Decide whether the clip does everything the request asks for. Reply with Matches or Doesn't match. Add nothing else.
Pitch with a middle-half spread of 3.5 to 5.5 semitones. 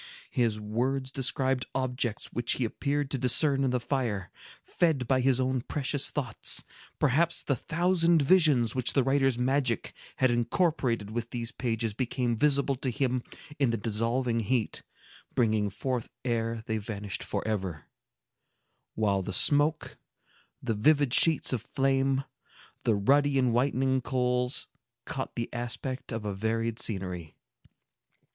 Doesn't match